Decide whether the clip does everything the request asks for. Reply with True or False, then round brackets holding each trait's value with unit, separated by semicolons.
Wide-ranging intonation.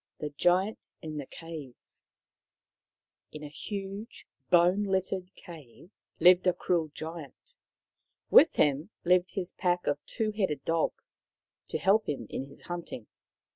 False (3.9 semitones)